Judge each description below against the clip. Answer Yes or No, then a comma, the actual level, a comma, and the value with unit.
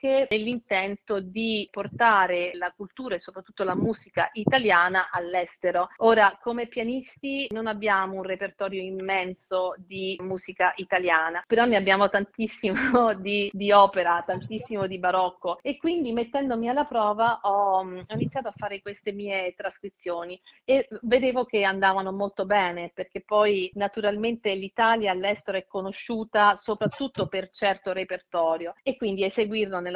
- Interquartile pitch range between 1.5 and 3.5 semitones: Yes, average, 2.9 semitones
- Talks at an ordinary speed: Yes, average, 130 wpm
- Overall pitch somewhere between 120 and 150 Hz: No, high, 200 Hz